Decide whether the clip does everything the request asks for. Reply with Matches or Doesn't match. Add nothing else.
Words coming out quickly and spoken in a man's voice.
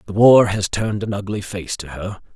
Matches